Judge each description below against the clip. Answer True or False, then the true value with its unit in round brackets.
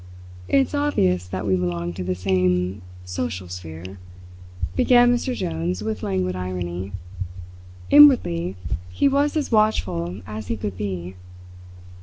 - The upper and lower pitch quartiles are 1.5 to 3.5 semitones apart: False (4.2 semitones)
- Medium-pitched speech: False (95 Hz)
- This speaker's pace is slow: True (125 wpm)